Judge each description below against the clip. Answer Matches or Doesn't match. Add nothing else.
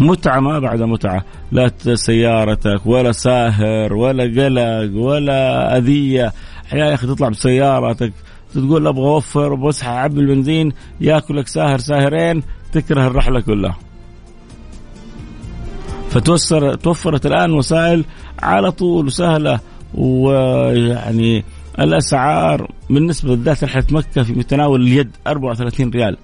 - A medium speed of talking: Matches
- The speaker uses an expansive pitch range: Doesn't match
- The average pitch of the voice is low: Matches